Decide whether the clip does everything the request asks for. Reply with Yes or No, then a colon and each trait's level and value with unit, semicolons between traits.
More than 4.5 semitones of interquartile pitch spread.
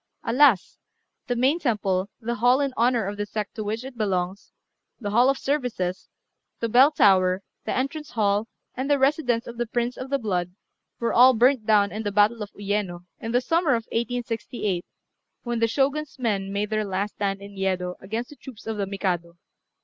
No: average, 3.9 semitones